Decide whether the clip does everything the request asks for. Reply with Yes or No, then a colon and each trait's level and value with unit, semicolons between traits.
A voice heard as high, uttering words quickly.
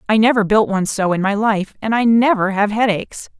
Yes: high, 210 Hz; fast, 230 wpm